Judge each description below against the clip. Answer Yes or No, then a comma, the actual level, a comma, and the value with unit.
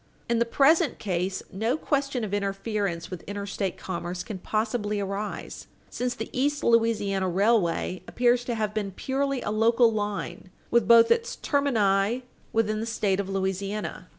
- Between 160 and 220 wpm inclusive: No, average, 150 wpm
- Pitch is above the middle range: Yes, high, 215 Hz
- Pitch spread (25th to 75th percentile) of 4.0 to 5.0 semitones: No, average, 3.3 semitones